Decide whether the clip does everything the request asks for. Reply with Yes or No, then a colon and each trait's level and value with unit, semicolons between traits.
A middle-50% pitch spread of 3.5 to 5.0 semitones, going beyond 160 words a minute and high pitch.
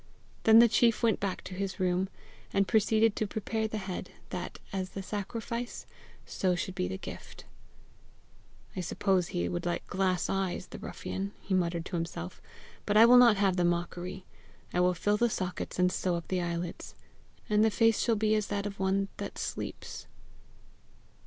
No: average, 3.0 semitones; average, 180 wpm; high, 195 Hz